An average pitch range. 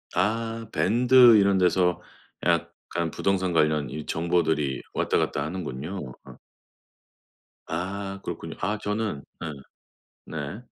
Yes: average, 4.8 semitones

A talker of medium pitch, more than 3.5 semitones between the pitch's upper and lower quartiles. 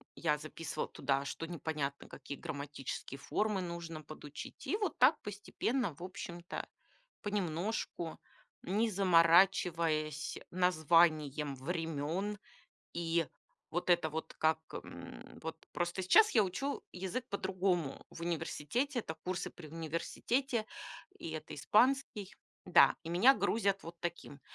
Yes: medium, 170 Hz; average, 4.0 semitones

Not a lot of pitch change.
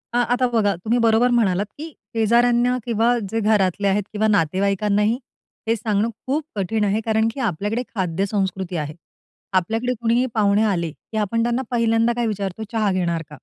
No: average, 3.1 semitones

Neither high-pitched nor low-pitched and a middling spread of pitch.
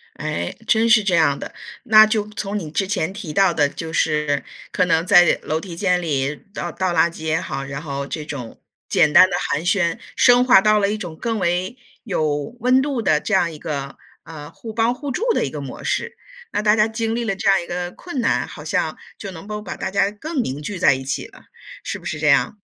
No: medium, 180 Hz; wide, 5.7 semitones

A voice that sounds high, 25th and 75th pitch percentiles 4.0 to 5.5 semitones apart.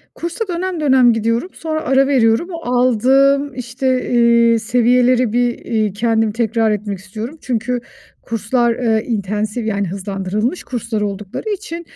No: high, 235 Hz; average, 3.3 semitones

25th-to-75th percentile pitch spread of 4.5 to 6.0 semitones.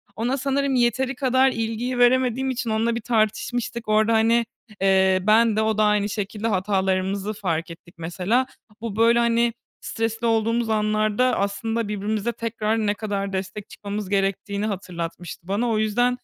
No: average, 2.7 semitones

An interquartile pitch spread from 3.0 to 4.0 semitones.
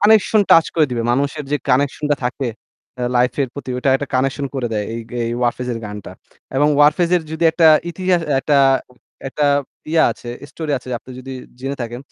Yes: average, 3.6 semitones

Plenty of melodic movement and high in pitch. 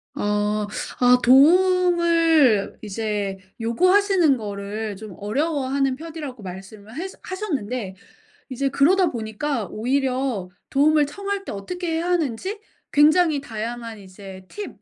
Yes: wide, 7.7 semitones; very high, 265 Hz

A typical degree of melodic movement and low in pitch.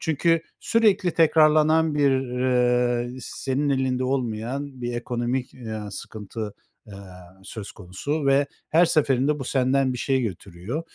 Yes: average, 3.5 semitones; low, 130 Hz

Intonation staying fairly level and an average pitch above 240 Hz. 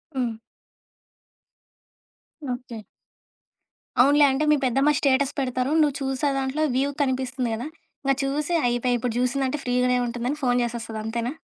Yes: narrow, 2.0 semitones; very high, 255 Hz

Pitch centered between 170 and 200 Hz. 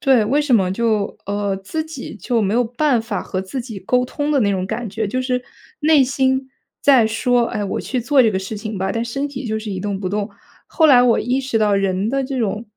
No: high, 230 Hz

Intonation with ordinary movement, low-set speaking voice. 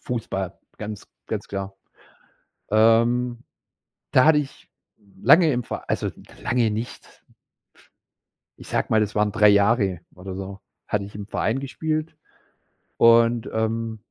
Yes: average, 3.1 semitones; low, 110 Hz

